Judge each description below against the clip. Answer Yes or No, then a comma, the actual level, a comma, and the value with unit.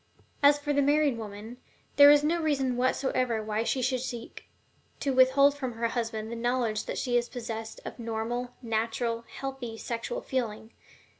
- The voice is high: Yes, high, 245 Hz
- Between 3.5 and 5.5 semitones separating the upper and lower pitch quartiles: No, average, 3.0 semitones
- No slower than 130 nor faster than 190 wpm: Yes, average, 165 wpm